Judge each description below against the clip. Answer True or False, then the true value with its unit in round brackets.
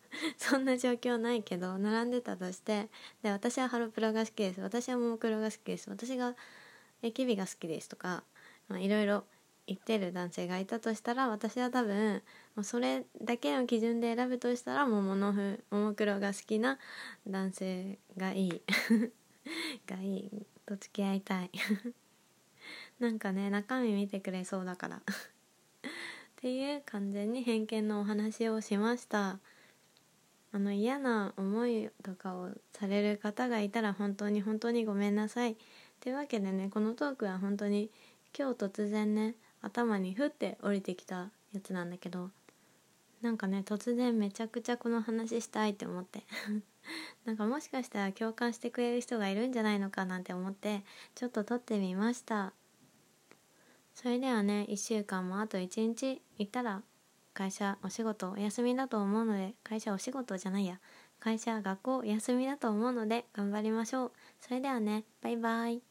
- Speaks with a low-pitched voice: False (215 Hz)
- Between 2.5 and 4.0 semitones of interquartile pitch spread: True (2.9 semitones)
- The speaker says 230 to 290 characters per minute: False (315 characters per minute)